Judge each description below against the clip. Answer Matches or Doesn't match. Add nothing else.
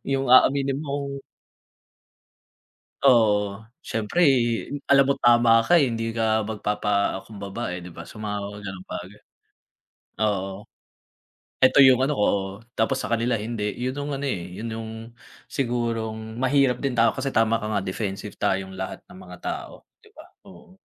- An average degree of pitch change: Matches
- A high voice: Doesn't match